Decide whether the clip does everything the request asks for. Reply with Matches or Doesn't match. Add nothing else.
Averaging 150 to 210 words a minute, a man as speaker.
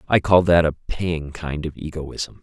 Matches